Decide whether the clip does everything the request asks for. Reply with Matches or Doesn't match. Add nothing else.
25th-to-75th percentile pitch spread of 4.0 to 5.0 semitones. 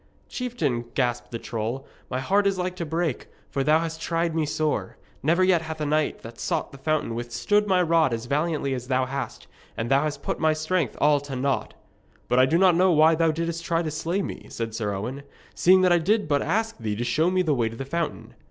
Matches